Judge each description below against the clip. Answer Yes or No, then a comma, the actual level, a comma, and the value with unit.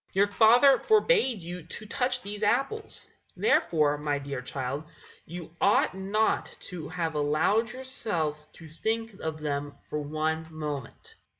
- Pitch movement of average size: No, wide, 6.6 semitones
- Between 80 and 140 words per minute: Yes, slow, 135 wpm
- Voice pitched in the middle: Yes, medium, 170 Hz